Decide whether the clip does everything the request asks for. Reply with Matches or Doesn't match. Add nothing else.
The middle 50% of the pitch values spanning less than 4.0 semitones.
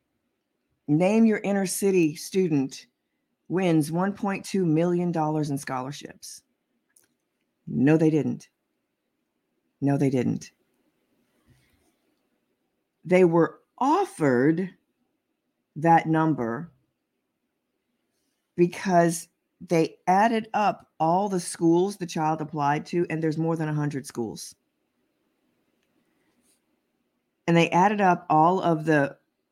Matches